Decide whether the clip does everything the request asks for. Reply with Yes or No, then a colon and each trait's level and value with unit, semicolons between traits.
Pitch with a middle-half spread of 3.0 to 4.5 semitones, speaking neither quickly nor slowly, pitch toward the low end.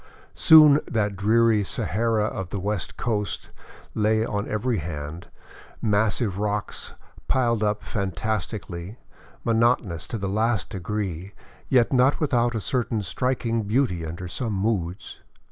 No: average, 3.3 semitones; slow, 125 wpm; low, 105 Hz